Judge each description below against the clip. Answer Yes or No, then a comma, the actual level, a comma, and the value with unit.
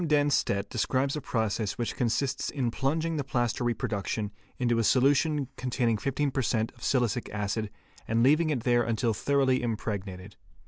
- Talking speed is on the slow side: No, average, 155 wpm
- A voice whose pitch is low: Yes, low, 120 Hz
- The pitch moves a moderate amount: Yes, average, 3.7 semitones